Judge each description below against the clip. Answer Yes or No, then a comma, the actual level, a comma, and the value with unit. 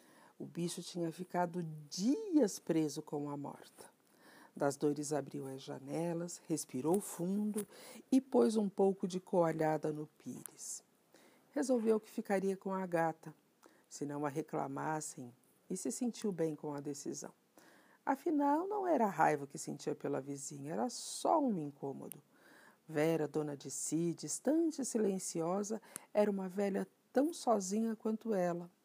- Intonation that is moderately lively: No, wide, 6.3 semitones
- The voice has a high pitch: No, medium, 175 Hz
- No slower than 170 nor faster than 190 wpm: No, average, 140 wpm